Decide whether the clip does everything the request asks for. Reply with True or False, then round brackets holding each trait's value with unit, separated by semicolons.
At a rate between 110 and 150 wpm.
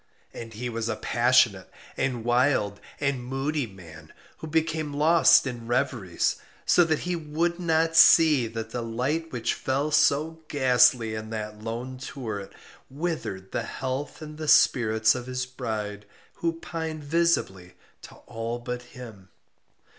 True (145 wpm)